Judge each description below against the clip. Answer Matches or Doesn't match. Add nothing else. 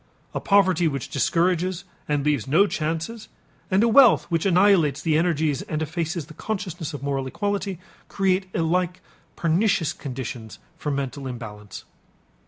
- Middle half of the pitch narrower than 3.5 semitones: Doesn't match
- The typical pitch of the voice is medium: Matches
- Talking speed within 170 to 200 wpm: Doesn't match